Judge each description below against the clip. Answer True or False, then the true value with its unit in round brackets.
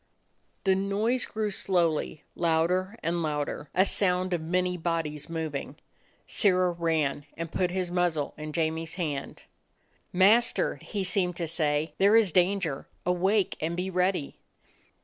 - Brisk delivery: False (140 wpm)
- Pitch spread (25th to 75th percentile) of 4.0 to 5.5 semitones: False (2.8 semitones)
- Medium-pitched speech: True (175 Hz)